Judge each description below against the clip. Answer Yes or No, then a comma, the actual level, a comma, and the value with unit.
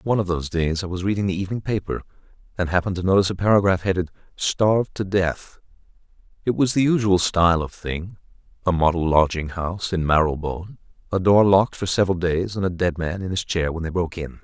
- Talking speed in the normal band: No, fast, 210 wpm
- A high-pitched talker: No, very low, 90 Hz